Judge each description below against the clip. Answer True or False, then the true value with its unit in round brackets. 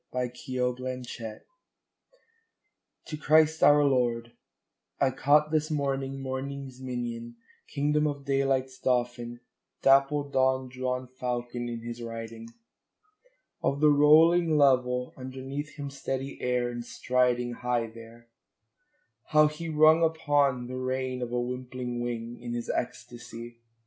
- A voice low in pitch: True (130 Hz)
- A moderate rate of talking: False (130 wpm)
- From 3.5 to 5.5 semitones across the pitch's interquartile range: False (2.6 semitones)